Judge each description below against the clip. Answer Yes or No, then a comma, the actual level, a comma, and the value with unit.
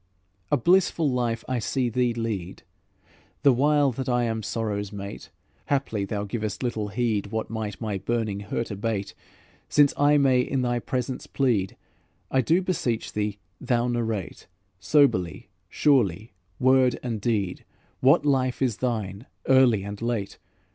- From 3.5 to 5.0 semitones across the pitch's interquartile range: Yes, average, 3.9 semitones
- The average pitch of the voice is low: Yes, low, 115 Hz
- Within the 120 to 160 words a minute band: Yes, average, 145 wpm